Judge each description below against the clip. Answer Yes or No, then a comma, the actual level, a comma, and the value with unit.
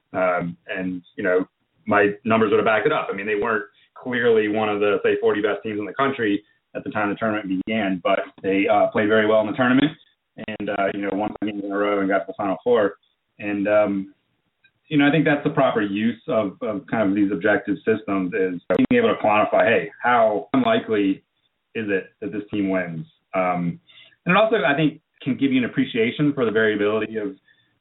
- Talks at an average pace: No, fast, 220 wpm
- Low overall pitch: Yes, low, 105 Hz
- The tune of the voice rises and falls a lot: Yes, wide, 6.5 semitones